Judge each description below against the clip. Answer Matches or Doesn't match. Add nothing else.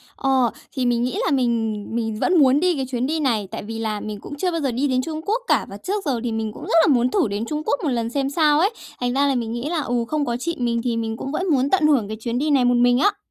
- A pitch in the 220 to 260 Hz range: Matches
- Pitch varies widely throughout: Doesn't match